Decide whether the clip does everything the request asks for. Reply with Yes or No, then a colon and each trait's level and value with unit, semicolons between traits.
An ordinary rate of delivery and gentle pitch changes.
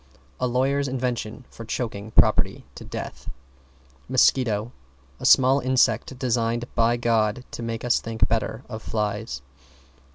No: slow, 130 wpm; narrow, 2.3 semitones